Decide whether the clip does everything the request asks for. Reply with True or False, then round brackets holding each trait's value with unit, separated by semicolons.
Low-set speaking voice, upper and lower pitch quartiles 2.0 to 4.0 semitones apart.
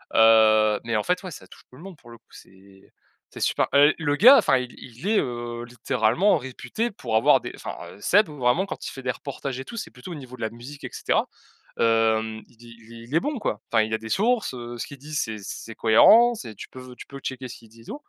False (125 Hz; 4.7 semitones)